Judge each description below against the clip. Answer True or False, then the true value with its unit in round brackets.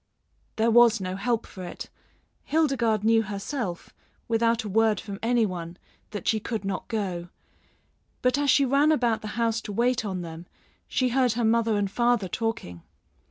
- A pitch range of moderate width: True (3.3 semitones)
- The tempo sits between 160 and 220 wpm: True (170 wpm)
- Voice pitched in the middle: False (225 Hz)